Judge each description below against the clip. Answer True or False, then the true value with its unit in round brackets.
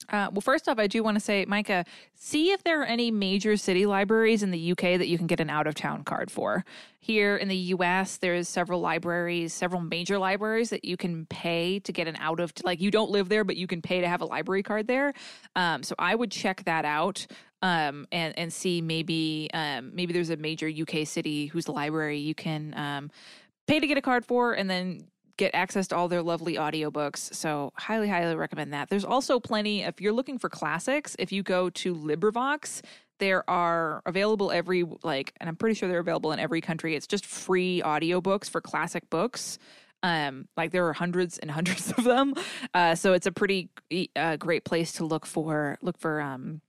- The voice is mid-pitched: True (180 Hz)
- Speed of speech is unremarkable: False (210 wpm)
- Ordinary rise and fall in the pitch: True (3.8 semitones)